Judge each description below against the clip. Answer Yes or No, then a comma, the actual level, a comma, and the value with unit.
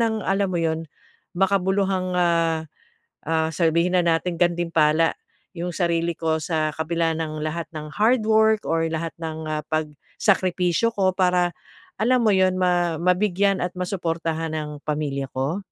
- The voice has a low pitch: No, medium, 170 Hz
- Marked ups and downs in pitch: No, average, 2.8 semitones